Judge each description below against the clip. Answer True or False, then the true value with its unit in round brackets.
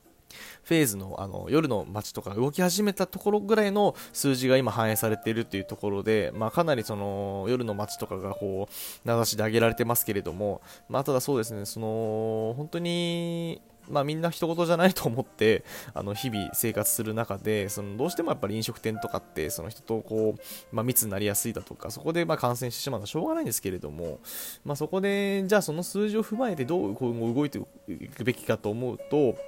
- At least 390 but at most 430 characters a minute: True (420 characters per minute)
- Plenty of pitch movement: True (6.9 semitones)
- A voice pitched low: True (115 Hz)